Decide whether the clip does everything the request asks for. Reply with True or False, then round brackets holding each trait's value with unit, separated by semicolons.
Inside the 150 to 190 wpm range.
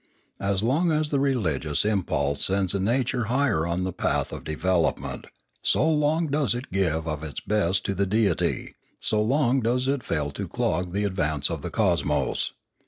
True (175 wpm)